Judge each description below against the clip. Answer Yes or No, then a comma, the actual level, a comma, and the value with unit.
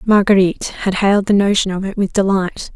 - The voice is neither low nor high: No, high, 195 Hz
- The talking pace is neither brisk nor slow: Yes, average, 195 wpm